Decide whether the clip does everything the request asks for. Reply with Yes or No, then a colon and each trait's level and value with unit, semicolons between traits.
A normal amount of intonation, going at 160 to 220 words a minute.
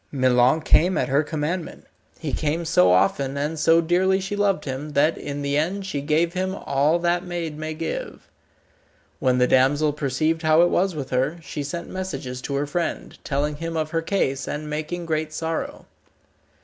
Yes: average, 3.3 semitones; average, 185 wpm